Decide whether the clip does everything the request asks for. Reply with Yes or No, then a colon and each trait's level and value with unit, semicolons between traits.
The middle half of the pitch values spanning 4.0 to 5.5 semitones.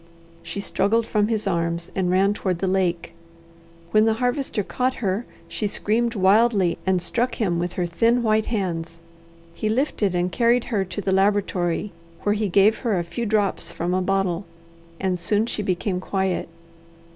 No: average, 3.3 semitones